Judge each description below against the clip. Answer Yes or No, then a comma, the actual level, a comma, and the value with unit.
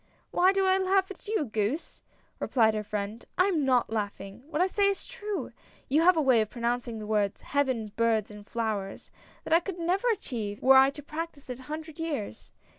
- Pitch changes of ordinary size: No, wide, 8.1 semitones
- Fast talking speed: Yes, fast, 225 wpm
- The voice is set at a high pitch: Yes, very high, 265 Hz